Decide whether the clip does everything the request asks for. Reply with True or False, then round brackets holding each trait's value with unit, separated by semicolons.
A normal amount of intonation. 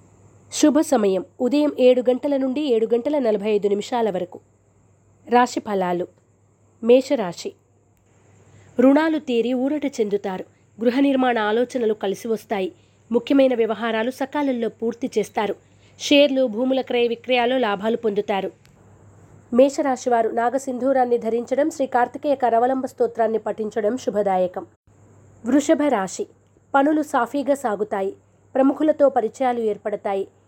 True (5.0 semitones)